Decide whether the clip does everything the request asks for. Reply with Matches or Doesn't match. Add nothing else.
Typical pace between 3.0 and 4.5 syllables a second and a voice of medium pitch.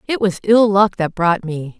Doesn't match